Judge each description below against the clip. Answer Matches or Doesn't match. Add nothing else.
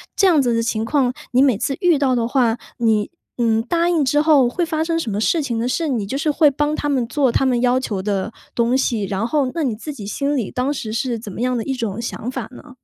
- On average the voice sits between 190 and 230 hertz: Doesn't match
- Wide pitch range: Doesn't match